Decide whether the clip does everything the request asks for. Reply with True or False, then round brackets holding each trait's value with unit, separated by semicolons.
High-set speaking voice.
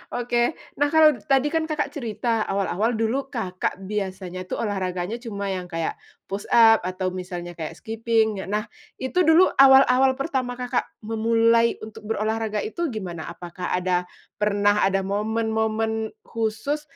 True (220 Hz)